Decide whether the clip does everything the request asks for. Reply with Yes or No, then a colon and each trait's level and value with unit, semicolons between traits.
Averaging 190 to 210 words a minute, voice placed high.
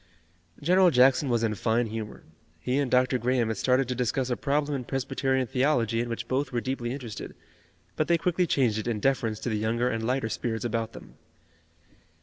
No: average, 195 wpm; low, 125 Hz